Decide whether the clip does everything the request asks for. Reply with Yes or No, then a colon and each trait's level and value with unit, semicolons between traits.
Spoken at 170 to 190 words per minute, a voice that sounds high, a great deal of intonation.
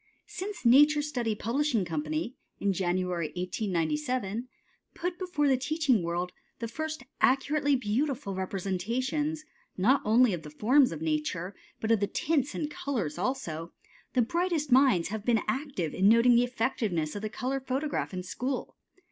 No: average, 150 wpm; high, 235 Hz; wide, 7.2 semitones